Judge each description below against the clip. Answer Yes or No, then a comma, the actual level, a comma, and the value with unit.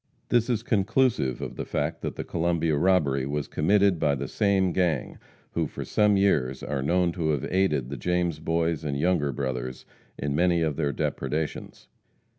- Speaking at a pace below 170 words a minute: No, average, 175 wpm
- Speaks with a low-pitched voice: Yes, very low, 80 Hz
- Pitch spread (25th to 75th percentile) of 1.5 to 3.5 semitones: No, average, 4.5 semitones